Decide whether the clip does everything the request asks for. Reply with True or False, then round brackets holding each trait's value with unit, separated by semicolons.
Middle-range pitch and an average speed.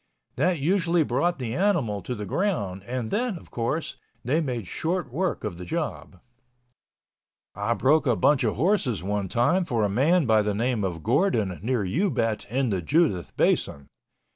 False (125 Hz; 170 wpm)